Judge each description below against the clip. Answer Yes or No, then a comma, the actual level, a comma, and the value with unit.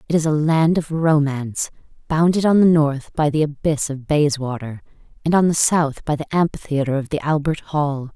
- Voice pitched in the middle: Yes, medium, 150 Hz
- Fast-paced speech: No, average, 190 wpm